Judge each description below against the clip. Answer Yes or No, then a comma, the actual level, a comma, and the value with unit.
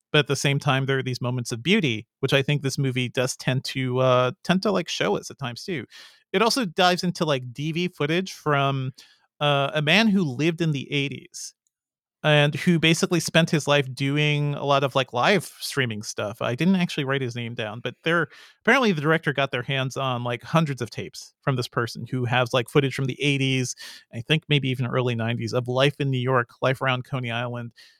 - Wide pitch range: No, average, 3.4 semitones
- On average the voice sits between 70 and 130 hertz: No, medium, 140 Hz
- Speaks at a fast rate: Yes, fast, 220 wpm